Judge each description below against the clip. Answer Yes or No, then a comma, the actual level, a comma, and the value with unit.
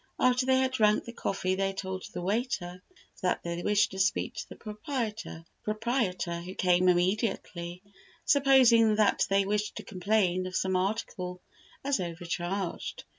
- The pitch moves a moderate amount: Yes, average, 3.7 semitones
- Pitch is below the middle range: No, high, 195 Hz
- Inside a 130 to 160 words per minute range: Yes, average, 145 wpm